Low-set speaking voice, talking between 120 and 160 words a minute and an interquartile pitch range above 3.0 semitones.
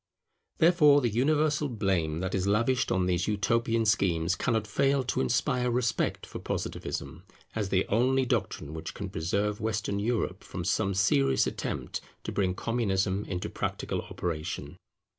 Yes: low, 105 Hz; average, 145 wpm; average, 4.7 semitones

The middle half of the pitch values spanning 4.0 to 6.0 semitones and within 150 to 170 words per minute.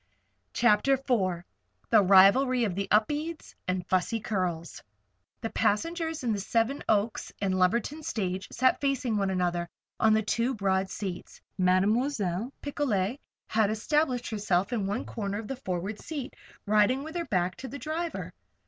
Yes: wide, 5.4 semitones; average, 155 wpm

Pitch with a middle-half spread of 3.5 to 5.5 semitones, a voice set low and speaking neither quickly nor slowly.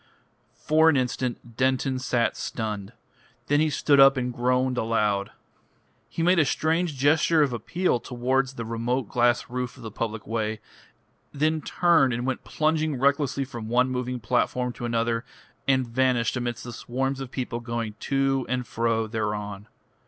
No: average, 2.7 semitones; low, 125 Hz; average, 160 wpm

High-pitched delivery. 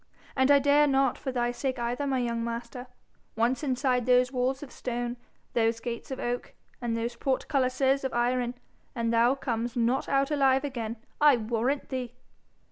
Yes: very high, 250 Hz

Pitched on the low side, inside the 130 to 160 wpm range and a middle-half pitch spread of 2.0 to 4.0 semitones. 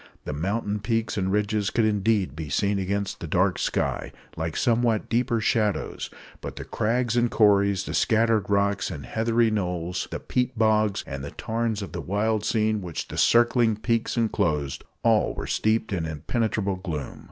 No: low, 105 Hz; average, 170 wpm; average, 3.1 semitones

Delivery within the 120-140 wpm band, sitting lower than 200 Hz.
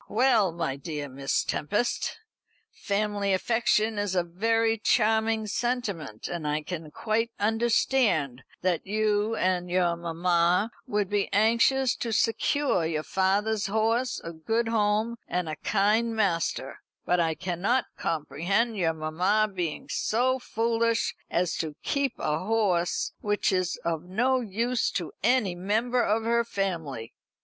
No: slow, 135 wpm; high, 205 Hz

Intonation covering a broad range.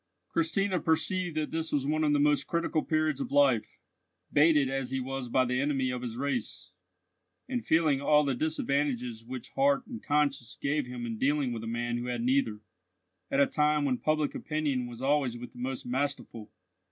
No: average, 3.6 semitones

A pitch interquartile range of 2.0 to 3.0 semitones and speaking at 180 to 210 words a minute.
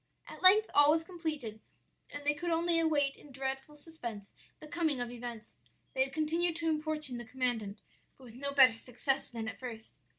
No: average, 4.6 semitones; average, 190 wpm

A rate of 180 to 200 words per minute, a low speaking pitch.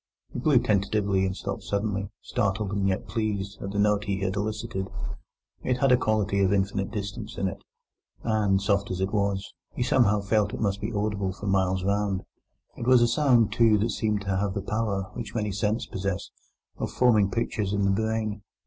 Yes: average, 195 wpm; low, 100 Hz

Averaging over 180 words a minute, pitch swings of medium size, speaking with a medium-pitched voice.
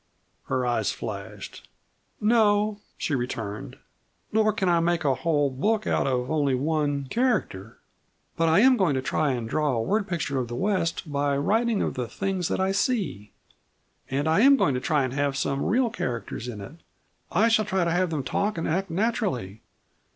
No: average, 190 wpm; wide, 7.7 semitones; medium, 160 Hz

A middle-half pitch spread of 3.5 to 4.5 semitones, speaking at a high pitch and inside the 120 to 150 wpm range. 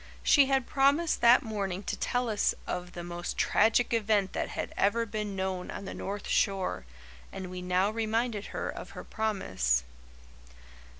No: average, 3.8 semitones; high, 205 Hz; average, 165 wpm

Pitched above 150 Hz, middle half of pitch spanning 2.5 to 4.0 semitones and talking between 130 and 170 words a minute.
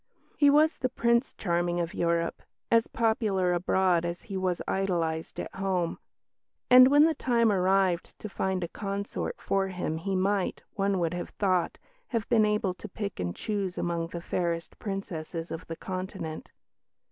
Yes: high, 190 Hz; average, 3.4 semitones; average, 165 wpm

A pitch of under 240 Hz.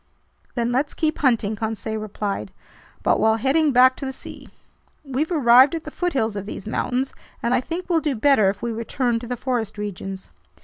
No: high, 245 Hz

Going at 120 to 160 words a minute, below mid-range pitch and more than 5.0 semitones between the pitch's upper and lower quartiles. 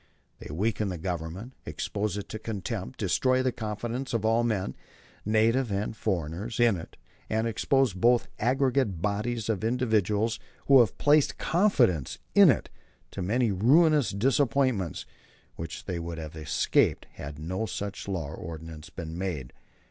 Yes: average, 150 wpm; low, 105 Hz; wide, 5.4 semitones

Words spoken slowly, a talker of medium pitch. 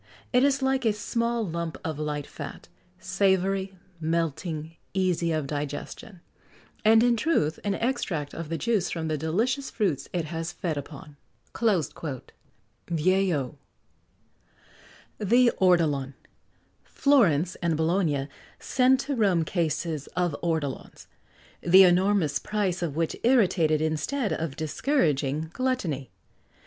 Yes: slow, 115 wpm; medium, 175 Hz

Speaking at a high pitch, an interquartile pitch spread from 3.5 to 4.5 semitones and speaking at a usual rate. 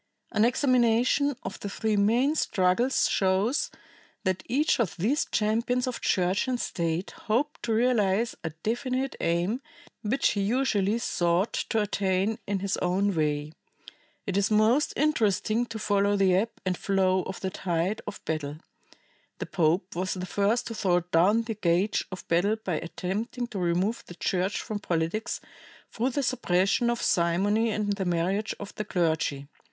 Yes: high, 200 Hz; average, 4.1 semitones; average, 160 wpm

